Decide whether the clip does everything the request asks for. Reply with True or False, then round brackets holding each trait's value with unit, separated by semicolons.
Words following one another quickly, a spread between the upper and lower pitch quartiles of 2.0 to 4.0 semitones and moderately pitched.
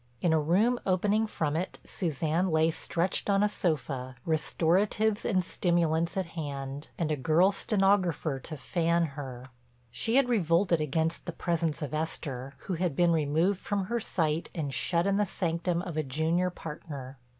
False (165 wpm; 3.5 semitones; 165 Hz)